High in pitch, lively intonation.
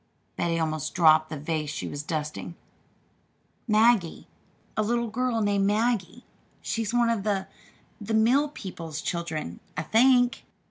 Yes: high, 200 Hz; wide, 6.4 semitones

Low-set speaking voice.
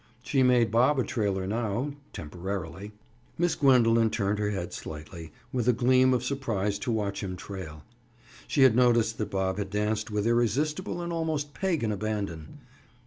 Yes: low, 110 Hz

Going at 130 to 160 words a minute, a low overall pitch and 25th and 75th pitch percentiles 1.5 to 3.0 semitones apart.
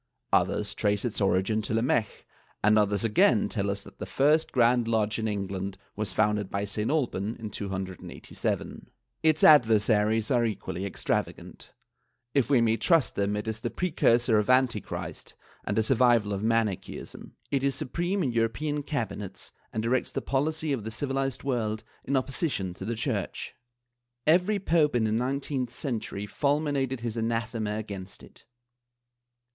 No: average, 155 wpm; low, 115 Hz; average, 4.4 semitones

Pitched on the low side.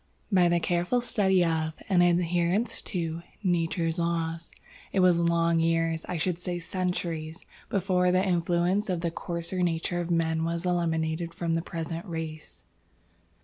No: medium, 170 Hz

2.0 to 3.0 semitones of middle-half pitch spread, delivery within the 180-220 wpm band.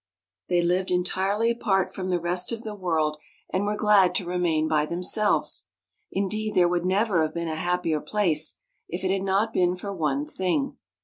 Yes: average, 2.7 semitones; average, 195 wpm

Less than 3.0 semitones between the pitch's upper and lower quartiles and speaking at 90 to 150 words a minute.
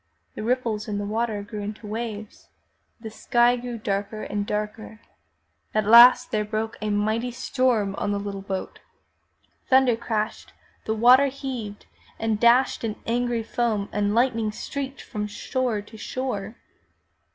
Yes: narrow, 2.5 semitones; average, 145 wpm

